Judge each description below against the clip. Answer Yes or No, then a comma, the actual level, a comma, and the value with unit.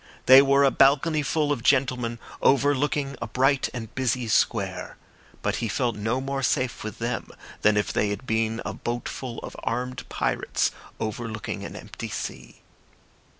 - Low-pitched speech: Yes, low, 125 Hz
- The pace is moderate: Yes, average, 150 wpm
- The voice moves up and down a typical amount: Yes, average, 3.1 semitones